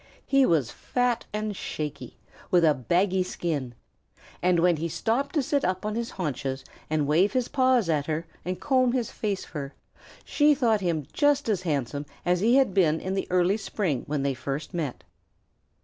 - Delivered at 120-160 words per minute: No, average, 180 wpm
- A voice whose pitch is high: No, medium, 180 Hz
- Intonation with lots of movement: Yes, wide, 7.2 semitones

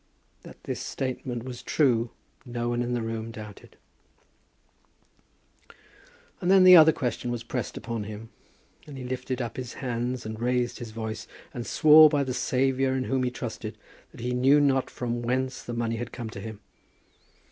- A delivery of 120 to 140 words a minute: No, average, 175 wpm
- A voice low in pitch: Yes, low, 125 Hz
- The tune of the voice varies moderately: No, narrow, 2.1 semitones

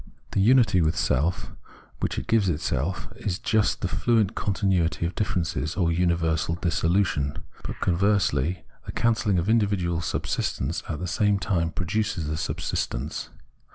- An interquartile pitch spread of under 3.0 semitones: No, average, 3.7 semitones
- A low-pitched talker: Yes, very low, 90 Hz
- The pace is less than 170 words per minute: Yes, average, 145 wpm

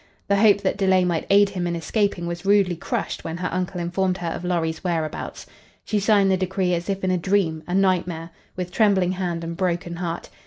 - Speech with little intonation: Yes, narrow, 2.1 semitones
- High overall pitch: No, medium, 180 Hz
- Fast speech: Yes, fast, 210 wpm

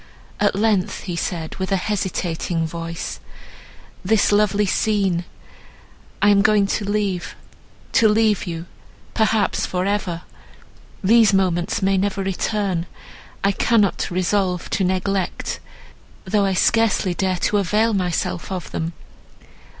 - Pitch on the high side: Yes, high, 195 Hz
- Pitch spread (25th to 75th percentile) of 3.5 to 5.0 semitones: No, narrow, 2.5 semitones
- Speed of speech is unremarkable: No, slow, 115 wpm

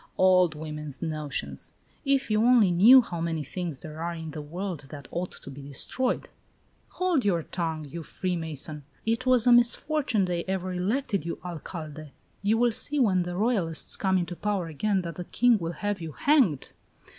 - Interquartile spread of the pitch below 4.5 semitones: No, average, 5.2 semitones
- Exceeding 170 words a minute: Yes, average, 180 wpm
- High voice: No, medium, 180 Hz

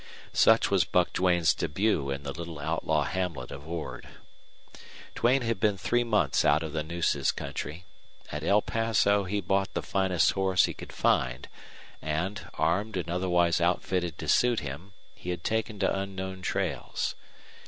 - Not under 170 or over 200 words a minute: No, average, 160 wpm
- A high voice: No, very low, 90 Hz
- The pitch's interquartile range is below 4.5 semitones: Yes, average, 3.7 semitones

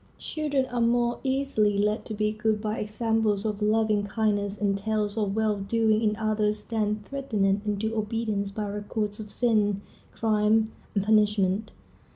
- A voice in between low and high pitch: No, high, 215 Hz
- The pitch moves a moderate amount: No, narrow, 1.3 semitones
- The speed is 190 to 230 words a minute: No, average, 155 wpm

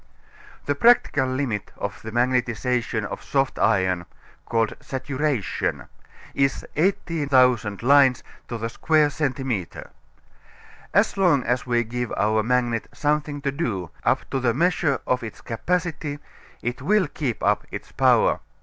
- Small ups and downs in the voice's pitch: No, average, 4.0 semitones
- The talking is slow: Yes, slow, 130 wpm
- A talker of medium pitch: No, low, 130 Hz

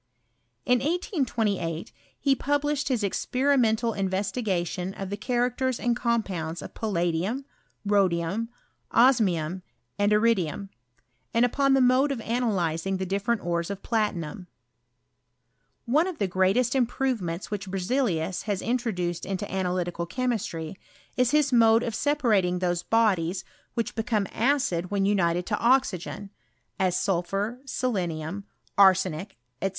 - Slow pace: Yes, slow, 125 wpm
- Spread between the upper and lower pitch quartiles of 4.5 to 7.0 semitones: Yes, average, 5.2 semitones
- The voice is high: Yes, high, 205 Hz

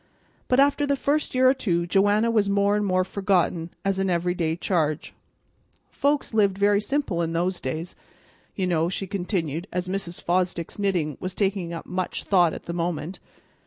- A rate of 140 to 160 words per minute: No, average, 175 wpm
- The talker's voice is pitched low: No, medium, 185 Hz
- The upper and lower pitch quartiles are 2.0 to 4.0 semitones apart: Yes, average, 3.1 semitones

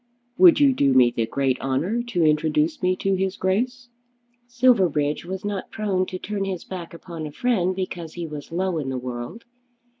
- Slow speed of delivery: No, average, 185 wpm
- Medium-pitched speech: Yes, medium, 180 Hz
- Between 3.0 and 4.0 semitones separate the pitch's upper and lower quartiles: No, average, 5.2 semitones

